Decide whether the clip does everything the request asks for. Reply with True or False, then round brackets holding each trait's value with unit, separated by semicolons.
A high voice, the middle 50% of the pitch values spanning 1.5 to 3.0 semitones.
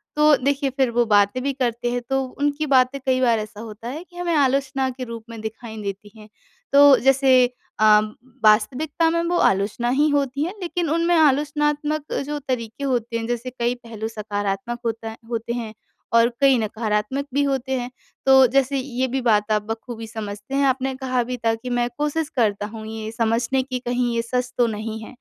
False (250 Hz; 3.5 semitones)